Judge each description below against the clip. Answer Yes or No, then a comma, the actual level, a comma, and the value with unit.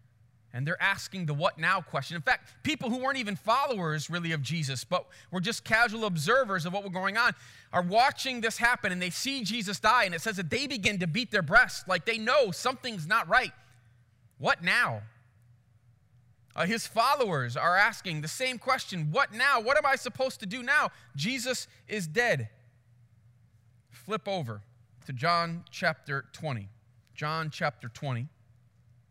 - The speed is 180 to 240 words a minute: No, average, 170 wpm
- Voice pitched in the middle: Yes, medium, 170 Hz